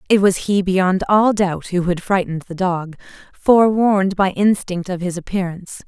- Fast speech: No, average, 175 wpm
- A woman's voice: Yes, female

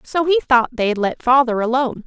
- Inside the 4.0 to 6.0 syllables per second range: Yes, 5.5 syllables/s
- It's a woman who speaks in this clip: Yes, female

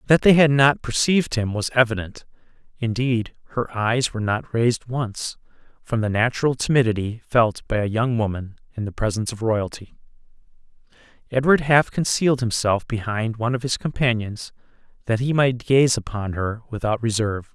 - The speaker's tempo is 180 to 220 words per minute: No, average, 155 wpm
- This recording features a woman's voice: No, male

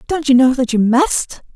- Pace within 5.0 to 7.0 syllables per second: No, 4.6 syllables/s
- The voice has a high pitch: Yes, very high, 265 Hz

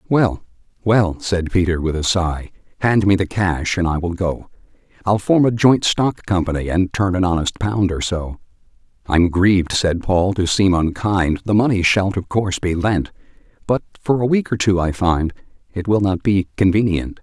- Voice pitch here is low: Yes, very low, 95 Hz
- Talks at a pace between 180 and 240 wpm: Yes, average, 190 wpm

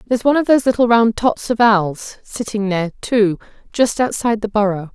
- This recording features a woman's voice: Yes, female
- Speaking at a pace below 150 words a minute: No, average, 195 wpm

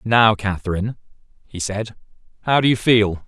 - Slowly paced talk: Yes, slow, 130 wpm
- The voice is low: Yes, low, 105 Hz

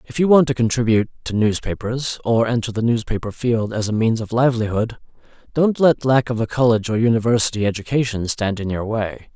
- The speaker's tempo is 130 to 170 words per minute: No, average, 190 wpm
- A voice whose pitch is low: Yes, low, 115 Hz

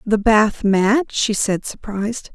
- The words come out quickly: No, average, 155 wpm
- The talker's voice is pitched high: Yes, high, 215 Hz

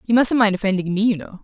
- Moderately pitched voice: No, high, 205 Hz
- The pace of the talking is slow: No, fast, 295 wpm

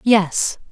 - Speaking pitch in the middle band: No, high, 200 Hz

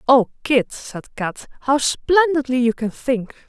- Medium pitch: No, very high, 260 Hz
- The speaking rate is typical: Yes, average, 155 wpm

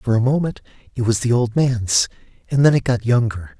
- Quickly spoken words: Yes, fast, 215 wpm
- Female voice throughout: No, male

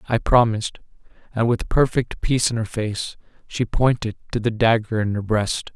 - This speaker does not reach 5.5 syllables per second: Yes, 5.0 syllables/s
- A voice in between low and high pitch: No, low, 115 Hz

